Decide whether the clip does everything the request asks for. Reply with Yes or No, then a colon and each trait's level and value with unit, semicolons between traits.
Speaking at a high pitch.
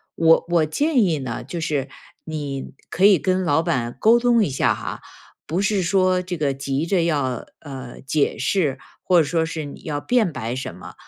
No: medium, 160 Hz